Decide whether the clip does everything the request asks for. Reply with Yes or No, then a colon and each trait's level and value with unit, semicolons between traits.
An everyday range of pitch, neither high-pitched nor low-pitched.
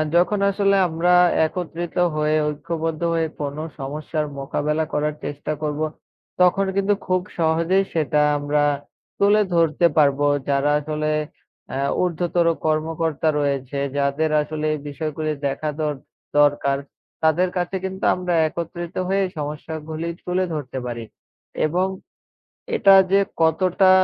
Yes: average, 3.1 semitones; medium, 155 Hz